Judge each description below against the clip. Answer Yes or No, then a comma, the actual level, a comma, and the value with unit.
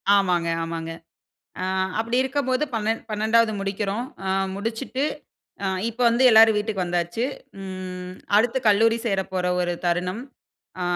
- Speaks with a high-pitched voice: Yes, high, 210 Hz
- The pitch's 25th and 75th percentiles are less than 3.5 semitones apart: No, average, 3.8 semitones